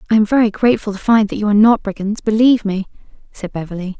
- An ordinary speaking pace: No, fast, 225 wpm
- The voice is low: No, high, 210 Hz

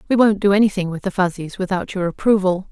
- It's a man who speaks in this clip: No, female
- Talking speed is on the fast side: Yes, fast, 220 wpm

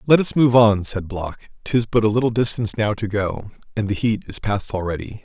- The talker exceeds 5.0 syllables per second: Yes, 5.4 syllables/s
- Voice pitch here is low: Yes, low, 105 Hz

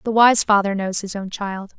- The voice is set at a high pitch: Yes, high, 205 Hz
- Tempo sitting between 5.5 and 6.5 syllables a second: No, 4.9 syllables/s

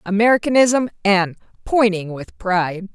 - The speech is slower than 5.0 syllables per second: Yes, 4.6 syllables/s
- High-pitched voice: Yes, high, 205 Hz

